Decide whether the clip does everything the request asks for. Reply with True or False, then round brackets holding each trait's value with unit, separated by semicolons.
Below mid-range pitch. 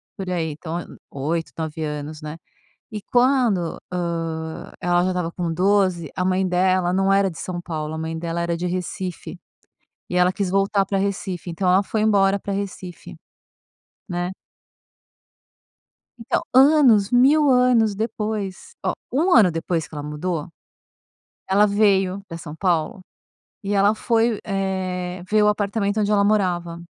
False (185 Hz)